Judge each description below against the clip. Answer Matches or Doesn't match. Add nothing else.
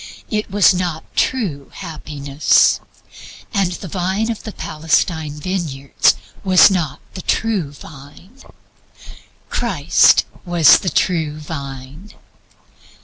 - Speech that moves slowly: Matches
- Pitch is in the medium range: Matches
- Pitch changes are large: Doesn't match